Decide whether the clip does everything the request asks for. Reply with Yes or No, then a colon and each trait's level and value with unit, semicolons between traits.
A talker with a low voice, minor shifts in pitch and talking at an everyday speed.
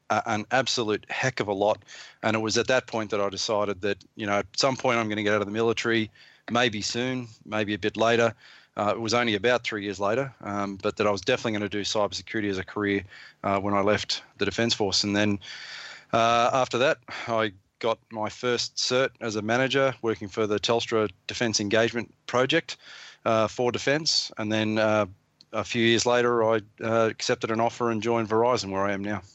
No: low, 110 Hz; narrow, 2.3 semitones; fast, 215 wpm